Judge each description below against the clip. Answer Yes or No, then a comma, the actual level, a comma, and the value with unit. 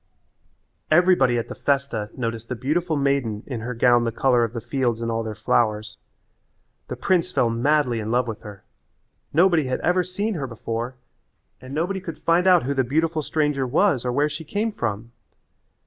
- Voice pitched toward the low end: Yes, low, 130 Hz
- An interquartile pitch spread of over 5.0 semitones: Yes, wide, 5.6 semitones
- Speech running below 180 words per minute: No, average, 185 wpm